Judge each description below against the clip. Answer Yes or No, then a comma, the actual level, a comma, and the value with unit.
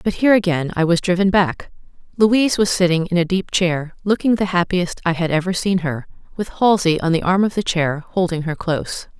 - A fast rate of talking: Yes, fast, 215 wpm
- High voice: No, medium, 180 Hz